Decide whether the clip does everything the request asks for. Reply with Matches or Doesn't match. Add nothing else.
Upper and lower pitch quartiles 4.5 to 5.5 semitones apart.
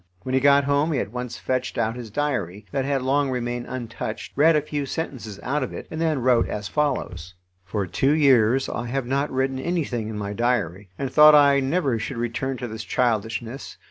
Doesn't match